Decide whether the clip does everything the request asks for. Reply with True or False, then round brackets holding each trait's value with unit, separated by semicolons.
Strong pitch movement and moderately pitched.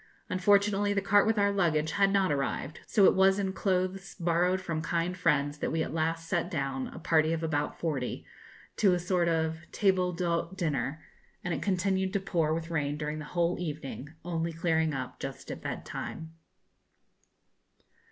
False (3.2 semitones; 170 Hz)